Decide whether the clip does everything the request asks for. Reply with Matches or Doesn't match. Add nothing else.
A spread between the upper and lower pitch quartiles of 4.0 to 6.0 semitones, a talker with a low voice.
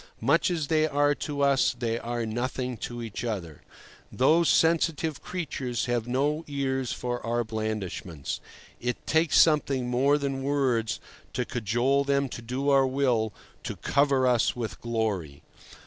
Doesn't match